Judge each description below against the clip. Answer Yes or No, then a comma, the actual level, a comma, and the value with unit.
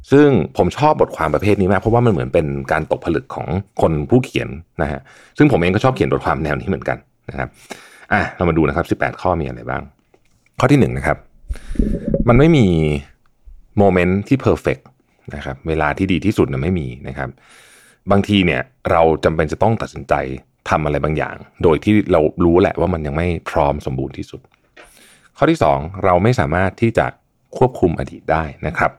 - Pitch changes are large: Yes, wide, 6.4 semitones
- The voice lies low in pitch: Yes, very low, 90 Hz